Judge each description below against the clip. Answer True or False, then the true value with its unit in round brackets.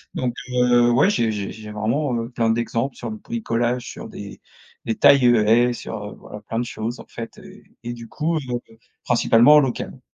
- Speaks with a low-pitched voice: True (120 Hz)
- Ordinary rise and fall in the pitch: False (1.8 semitones)